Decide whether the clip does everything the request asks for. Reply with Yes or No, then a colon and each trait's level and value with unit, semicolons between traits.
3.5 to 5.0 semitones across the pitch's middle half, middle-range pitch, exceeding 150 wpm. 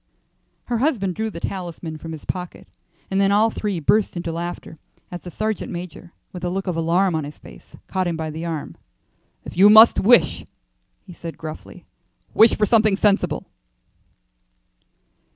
Yes: average, 3.8 semitones; medium, 180 Hz; average, 165 wpm